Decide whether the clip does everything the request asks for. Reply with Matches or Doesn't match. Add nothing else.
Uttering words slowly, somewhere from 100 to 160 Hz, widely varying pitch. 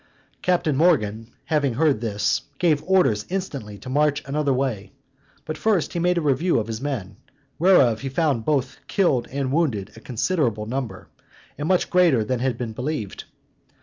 Doesn't match